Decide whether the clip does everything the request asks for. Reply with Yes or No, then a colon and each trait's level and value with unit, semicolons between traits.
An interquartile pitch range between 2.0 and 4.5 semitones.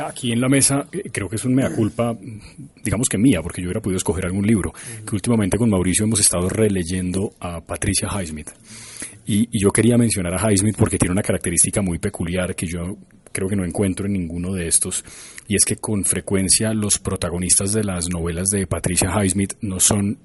Yes: average, 3.3 semitones